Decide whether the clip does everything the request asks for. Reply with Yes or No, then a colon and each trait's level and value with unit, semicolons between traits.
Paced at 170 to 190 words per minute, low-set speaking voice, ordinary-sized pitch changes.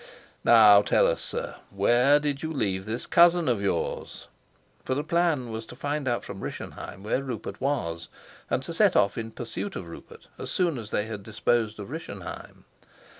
No: average, 180 wpm; low, 120 Hz; wide, 5.9 semitones